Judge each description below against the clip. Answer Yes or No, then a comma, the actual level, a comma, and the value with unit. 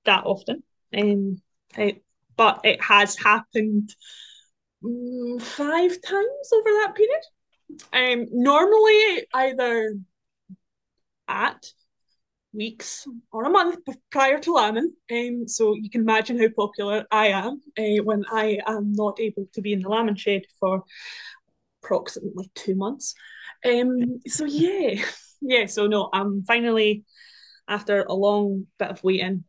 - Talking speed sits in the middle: No, slow, 125 wpm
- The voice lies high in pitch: Yes, high, 220 Hz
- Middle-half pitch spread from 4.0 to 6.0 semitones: Yes, average, 4.6 semitones